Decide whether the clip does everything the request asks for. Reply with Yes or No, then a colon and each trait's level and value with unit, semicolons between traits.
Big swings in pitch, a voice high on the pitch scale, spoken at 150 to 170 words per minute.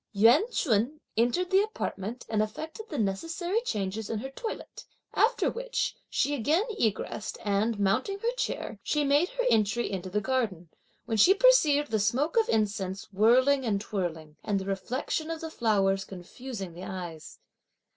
Yes: wide, 7.9 semitones; high, 225 Hz; average, 160 wpm